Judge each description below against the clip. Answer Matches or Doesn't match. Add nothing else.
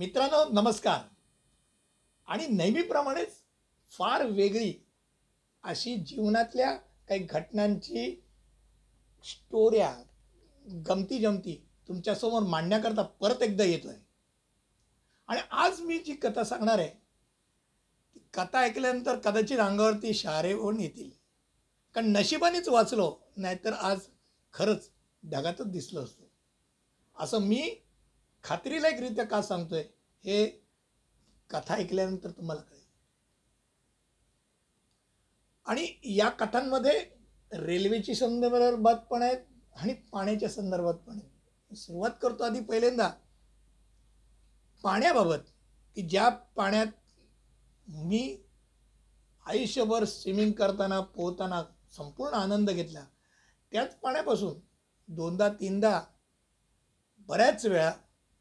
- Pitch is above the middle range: Matches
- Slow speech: Matches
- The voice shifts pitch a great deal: Doesn't match